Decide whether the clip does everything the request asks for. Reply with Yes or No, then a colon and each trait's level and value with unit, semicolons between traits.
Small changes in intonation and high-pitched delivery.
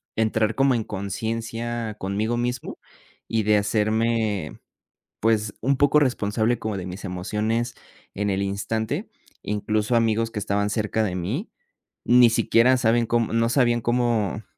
No: narrow, 2.3 semitones; low, 110 Hz